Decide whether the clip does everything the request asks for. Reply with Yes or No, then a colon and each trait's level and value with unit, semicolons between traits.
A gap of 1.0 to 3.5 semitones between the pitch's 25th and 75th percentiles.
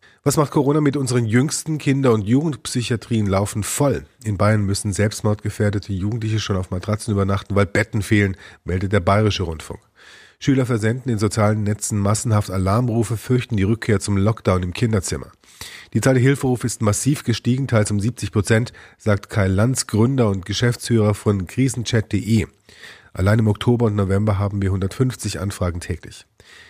Yes: average, 2.9 semitones